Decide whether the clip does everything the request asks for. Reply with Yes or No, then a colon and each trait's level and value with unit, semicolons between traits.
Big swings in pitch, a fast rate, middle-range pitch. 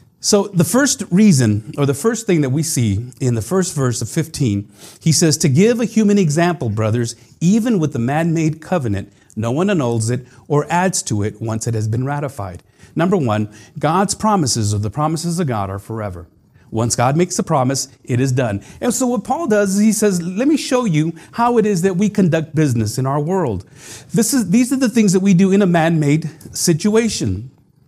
Yes: wide, 8.5 semitones; fast, 210 wpm; medium, 155 Hz